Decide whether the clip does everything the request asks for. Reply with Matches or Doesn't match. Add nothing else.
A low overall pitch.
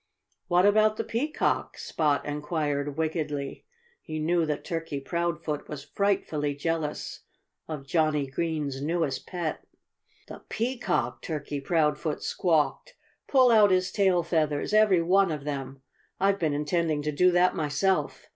Doesn't match